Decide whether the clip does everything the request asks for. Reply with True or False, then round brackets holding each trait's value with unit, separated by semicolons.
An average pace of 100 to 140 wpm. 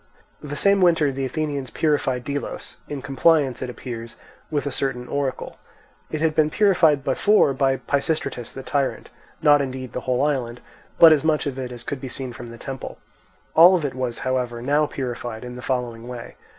False (190 wpm)